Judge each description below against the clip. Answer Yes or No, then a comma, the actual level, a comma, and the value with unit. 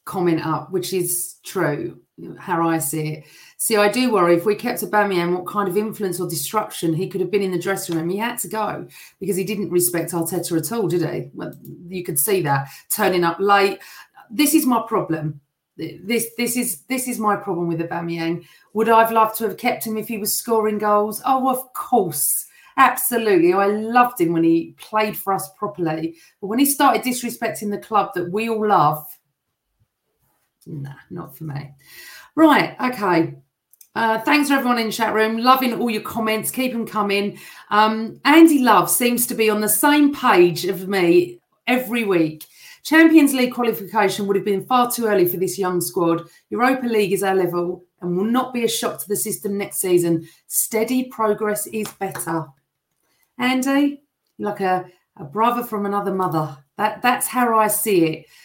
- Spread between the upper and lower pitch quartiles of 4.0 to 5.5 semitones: Yes, average, 4.8 semitones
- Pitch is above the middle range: Yes, high, 205 Hz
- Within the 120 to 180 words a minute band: No, average, 190 wpm